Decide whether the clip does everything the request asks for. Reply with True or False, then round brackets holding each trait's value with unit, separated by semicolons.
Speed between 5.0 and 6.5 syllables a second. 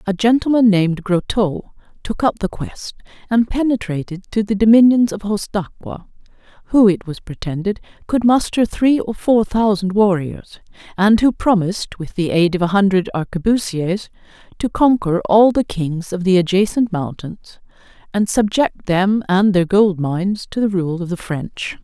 False (4.7 syllables/s)